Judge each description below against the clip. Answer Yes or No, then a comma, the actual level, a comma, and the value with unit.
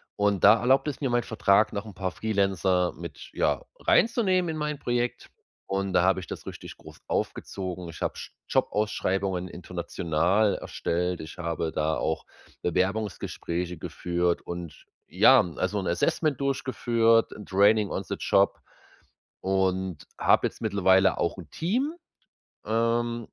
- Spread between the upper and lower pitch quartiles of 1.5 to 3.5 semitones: No, average, 4.4 semitones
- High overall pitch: No, very low, 95 Hz